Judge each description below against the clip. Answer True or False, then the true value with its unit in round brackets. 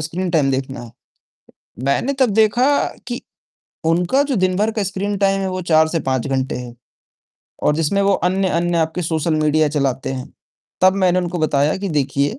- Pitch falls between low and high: True (170 Hz)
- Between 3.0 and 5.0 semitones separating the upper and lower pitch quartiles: False (5.4 semitones)